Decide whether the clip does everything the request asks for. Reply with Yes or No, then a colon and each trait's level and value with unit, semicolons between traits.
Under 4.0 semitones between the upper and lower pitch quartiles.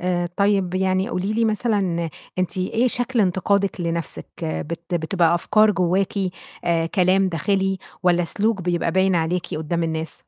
Yes: average, 2.7 semitones